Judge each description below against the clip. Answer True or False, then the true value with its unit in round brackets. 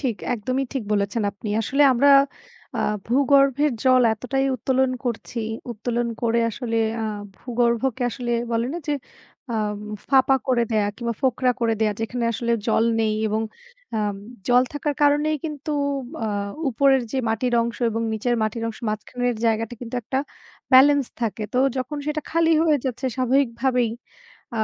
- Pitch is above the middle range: True (245 Hz)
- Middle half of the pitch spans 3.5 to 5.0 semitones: False (2.9 semitones)